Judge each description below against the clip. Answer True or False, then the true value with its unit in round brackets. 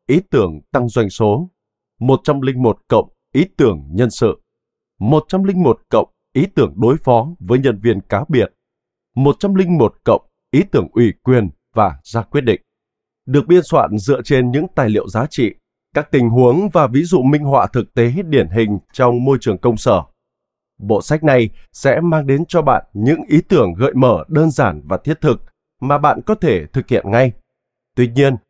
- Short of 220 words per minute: True (180 wpm)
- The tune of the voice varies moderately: True (4.8 semitones)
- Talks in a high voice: False (130 Hz)